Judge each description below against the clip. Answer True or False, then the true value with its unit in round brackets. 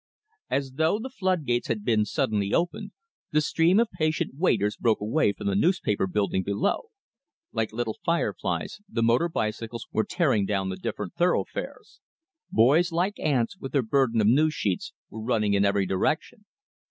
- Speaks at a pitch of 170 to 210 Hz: False (120 Hz)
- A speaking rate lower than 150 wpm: False (165 wpm)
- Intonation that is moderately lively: False (7.7 semitones)